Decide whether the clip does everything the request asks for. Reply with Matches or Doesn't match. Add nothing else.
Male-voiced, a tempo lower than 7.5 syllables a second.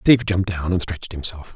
Matches